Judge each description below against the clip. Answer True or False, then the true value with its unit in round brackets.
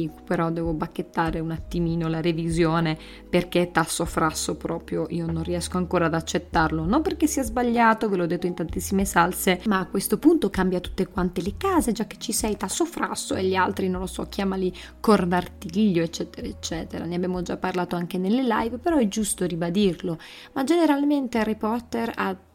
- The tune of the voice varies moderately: True (4.4 semitones)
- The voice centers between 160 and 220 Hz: True (185 Hz)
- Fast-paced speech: True (180 wpm)